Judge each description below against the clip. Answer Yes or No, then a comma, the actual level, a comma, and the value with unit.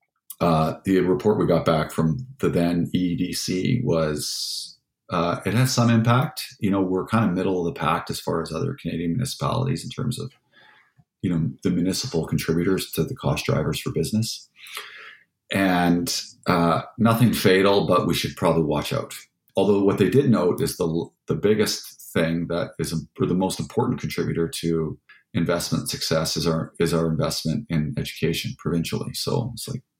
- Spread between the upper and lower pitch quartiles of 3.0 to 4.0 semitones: No, average, 4.9 semitones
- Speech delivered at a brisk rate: No, average, 175 wpm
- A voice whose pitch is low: Yes, very low, 90 Hz